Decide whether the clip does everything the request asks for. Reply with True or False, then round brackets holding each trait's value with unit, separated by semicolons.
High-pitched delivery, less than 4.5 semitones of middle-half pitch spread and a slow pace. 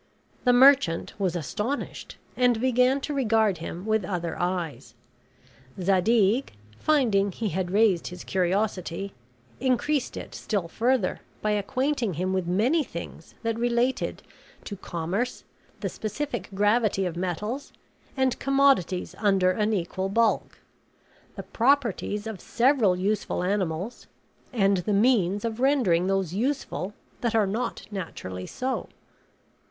False (210 Hz; 5.0 semitones; 125 wpm)